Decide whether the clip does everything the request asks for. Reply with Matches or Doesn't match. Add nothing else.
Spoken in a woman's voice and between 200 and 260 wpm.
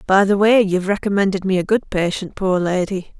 Matches